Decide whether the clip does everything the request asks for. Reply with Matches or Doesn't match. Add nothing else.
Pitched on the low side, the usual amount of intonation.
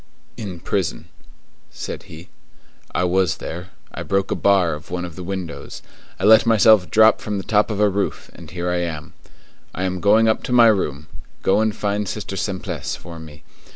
Matches